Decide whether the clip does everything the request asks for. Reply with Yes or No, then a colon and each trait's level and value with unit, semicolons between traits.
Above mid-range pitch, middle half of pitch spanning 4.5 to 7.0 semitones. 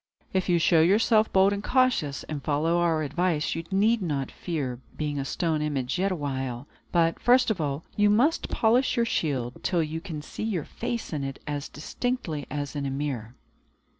No: medium, 160 Hz; wide, 5.5 semitones